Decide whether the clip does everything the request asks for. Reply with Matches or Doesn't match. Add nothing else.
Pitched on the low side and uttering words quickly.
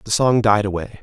Matches